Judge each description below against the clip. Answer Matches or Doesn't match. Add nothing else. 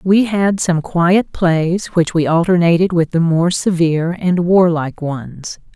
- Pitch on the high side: Doesn't match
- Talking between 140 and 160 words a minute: Matches